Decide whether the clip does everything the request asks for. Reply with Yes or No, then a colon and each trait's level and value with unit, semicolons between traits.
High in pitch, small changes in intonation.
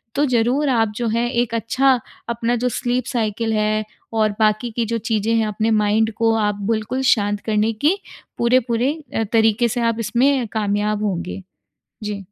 Yes: high, 225 Hz; narrow, 2.2 semitones